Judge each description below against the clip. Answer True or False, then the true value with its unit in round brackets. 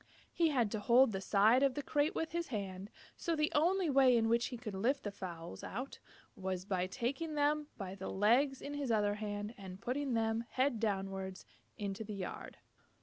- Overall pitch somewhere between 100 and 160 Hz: False (225 Hz)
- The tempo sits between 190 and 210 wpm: True (200 wpm)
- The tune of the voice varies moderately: False (5.8 semitones)